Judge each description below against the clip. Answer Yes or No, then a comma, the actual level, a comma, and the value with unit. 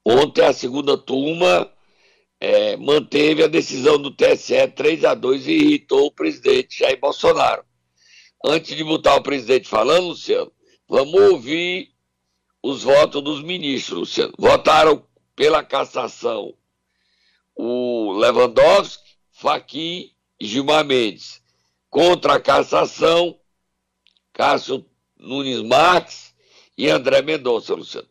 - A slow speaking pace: Yes, slow, 110 wpm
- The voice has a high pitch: No, medium, 175 Hz